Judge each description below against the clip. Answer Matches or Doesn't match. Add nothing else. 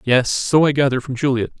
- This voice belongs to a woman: Doesn't match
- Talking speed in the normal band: Doesn't match